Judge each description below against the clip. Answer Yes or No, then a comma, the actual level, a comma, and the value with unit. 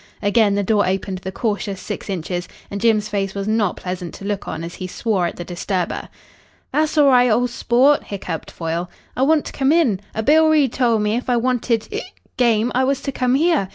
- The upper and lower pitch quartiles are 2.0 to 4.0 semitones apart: No, average, 4.9 semitones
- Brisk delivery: Yes, fast, 215 wpm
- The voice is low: No, high, 220 Hz